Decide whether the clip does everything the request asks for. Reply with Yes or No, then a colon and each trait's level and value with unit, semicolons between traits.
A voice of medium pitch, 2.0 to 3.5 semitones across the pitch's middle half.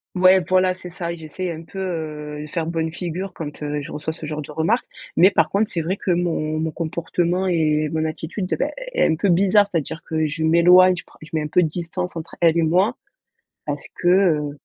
Yes: medium, 165 Hz; narrow, 2.6 semitones